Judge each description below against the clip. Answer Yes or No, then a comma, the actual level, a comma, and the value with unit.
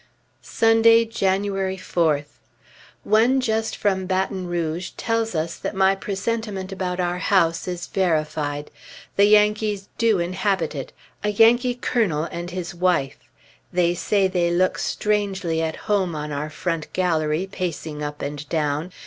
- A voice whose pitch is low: No, medium, 185 Hz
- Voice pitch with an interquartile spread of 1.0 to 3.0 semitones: No, average, 4.0 semitones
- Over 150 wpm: No, slow, 135 wpm